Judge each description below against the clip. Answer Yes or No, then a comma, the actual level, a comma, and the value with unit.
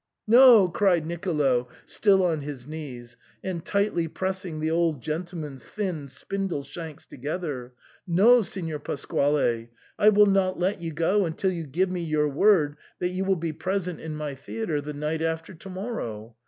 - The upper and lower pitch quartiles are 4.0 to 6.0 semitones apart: Yes, average, 4.3 semitones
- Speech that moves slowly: No, average, 175 wpm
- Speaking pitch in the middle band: Yes, medium, 165 Hz